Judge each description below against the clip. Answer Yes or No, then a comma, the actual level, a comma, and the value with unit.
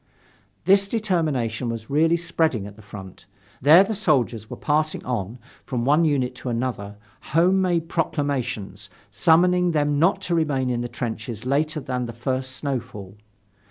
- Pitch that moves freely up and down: Yes, wide, 5.7 semitones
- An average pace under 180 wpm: Yes, average, 155 wpm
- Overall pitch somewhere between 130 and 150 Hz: Yes, low, 135 Hz